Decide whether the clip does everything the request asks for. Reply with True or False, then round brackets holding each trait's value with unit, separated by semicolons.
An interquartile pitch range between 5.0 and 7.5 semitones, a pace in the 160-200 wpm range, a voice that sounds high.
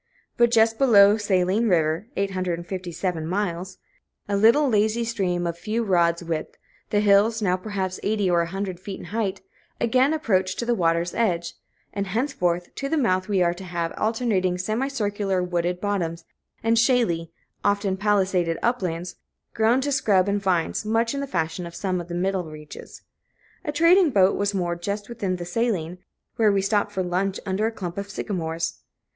False (3.8 semitones; 175 wpm; 195 Hz)